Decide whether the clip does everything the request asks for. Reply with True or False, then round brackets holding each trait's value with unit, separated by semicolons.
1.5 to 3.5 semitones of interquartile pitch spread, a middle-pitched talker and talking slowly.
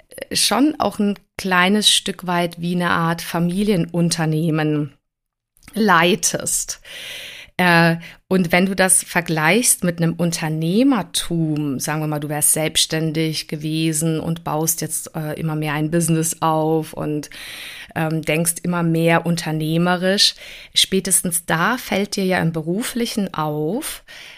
True (2.9 semitones; 165 Hz; 115 wpm)